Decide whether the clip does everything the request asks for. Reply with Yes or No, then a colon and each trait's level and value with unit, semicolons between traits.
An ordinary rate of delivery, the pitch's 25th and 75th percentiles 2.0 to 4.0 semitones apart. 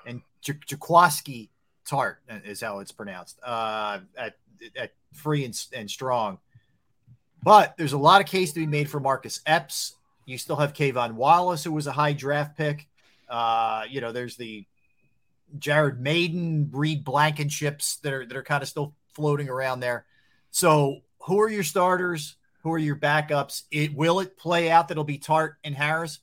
Yes: average, 175 wpm; average, 3.5 semitones